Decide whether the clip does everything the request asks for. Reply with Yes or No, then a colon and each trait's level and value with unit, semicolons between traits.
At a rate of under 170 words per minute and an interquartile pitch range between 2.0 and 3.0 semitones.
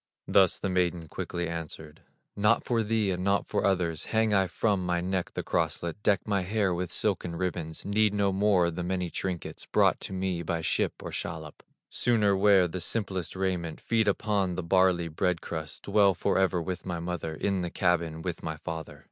No: average, 190 wpm; narrow, 2.6 semitones